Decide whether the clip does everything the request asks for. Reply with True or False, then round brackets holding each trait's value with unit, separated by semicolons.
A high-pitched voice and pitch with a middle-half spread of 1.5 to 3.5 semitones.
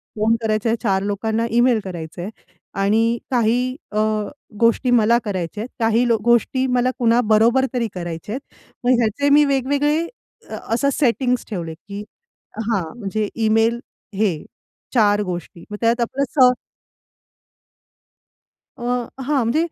True (230 Hz; 3.2 semitones)